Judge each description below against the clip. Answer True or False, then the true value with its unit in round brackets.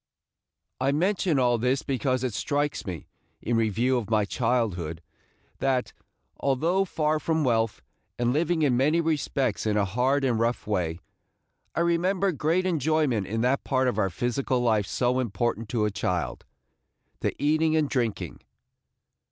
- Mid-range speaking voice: False (130 Hz)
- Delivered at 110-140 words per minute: False (155 wpm)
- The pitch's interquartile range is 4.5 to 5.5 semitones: True (5.2 semitones)